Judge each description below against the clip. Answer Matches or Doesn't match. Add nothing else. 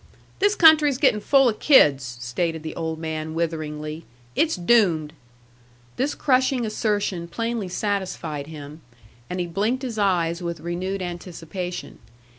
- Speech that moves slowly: Matches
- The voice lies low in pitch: Doesn't match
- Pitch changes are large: Matches